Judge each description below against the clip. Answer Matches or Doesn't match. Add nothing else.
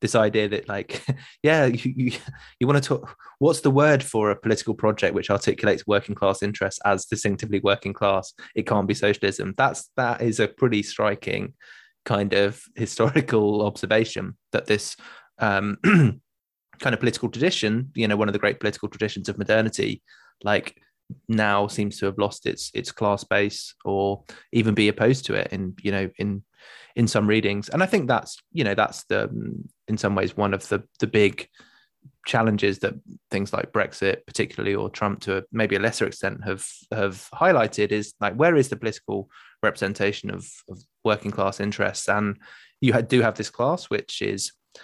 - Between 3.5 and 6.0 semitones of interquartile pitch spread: Doesn't match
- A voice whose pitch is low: Matches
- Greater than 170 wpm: Matches